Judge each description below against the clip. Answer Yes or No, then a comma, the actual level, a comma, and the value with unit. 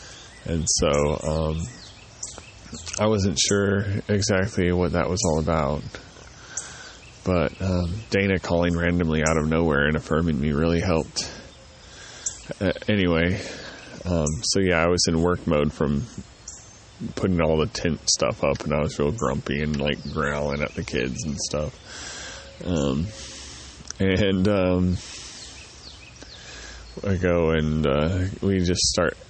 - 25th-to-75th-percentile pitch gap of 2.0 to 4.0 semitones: Yes, average, 3.6 semitones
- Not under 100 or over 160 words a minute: Yes, slow, 135 wpm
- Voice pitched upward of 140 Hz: No, very low, 85 Hz